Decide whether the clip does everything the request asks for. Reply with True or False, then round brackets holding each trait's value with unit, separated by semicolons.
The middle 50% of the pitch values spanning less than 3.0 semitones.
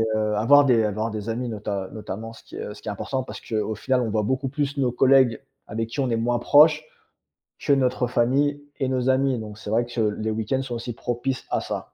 False (3.3 semitones)